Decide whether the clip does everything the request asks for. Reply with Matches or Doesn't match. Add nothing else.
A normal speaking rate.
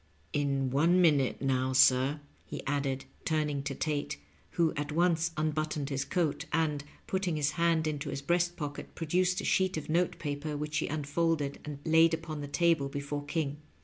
Matches